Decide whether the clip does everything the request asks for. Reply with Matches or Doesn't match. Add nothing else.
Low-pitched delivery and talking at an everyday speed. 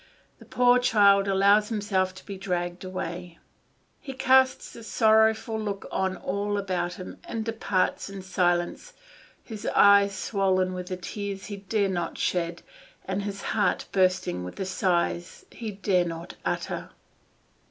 Doesn't match